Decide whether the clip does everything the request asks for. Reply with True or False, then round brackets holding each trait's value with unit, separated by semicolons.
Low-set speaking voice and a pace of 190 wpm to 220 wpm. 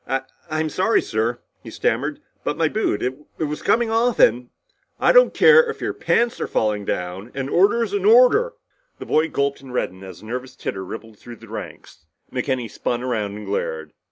True (130 Hz; 195 wpm)